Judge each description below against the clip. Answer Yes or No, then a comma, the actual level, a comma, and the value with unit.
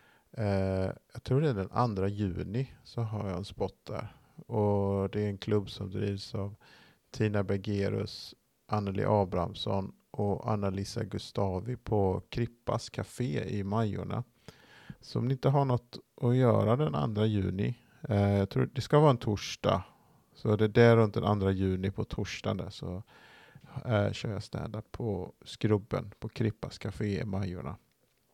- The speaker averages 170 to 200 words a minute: No, average, 160 wpm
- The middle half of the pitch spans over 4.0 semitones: No, average, 3.2 semitones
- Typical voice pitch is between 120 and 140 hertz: No, low, 105 Hz